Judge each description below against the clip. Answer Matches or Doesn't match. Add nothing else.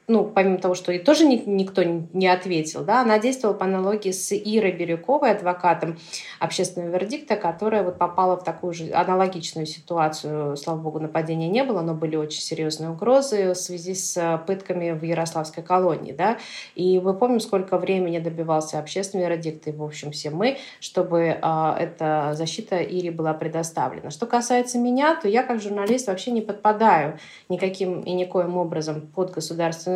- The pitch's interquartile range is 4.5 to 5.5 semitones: Doesn't match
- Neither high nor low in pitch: Matches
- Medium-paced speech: Doesn't match